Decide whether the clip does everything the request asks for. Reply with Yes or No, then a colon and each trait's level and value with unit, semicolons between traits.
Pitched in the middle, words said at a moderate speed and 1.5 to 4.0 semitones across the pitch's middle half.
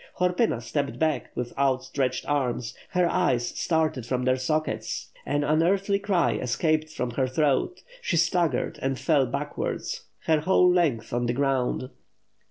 No: medium, 145 Hz; average, 155 wpm; average, 4.5 semitones